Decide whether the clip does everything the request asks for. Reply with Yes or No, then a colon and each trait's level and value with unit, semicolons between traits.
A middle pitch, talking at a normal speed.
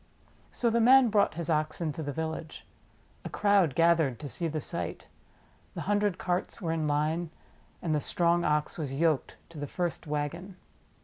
Yes: medium, 165 Hz; average, 175 wpm